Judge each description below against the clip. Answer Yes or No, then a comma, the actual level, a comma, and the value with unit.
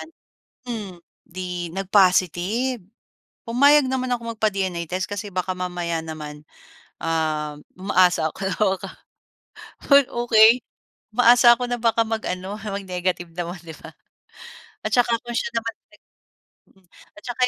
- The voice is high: Yes, high, 195 Hz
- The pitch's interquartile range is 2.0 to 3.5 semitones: No, average, 4.8 semitones